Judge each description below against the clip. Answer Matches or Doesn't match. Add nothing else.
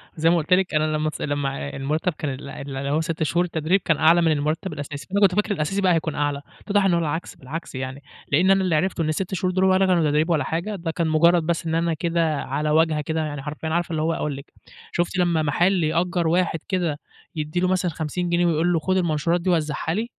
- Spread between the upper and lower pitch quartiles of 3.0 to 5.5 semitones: Doesn't match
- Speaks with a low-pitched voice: Doesn't match